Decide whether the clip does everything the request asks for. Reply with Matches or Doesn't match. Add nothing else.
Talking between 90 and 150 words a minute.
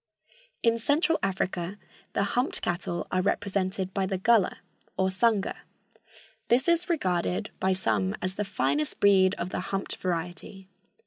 Matches